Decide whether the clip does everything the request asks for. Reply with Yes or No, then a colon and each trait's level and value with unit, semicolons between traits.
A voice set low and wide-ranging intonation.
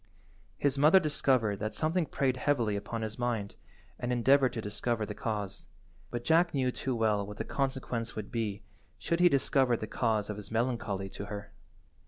No: low, 115 Hz; average, 4.2 semitones